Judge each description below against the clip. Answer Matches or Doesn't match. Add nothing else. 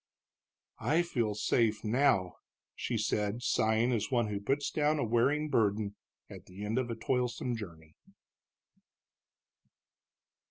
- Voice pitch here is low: Matches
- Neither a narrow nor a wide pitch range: Matches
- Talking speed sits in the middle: Doesn't match